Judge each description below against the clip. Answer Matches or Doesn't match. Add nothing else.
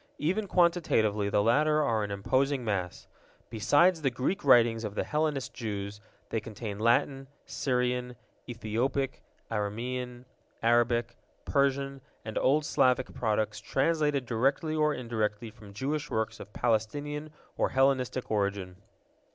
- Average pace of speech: Doesn't match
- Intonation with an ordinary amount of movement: Matches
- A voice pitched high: Doesn't match